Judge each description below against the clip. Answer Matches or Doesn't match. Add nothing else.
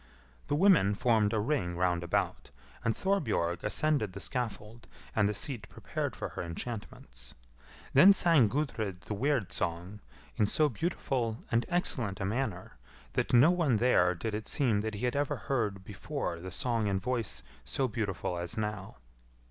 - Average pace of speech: Matches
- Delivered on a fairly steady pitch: Doesn't match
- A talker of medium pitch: Doesn't match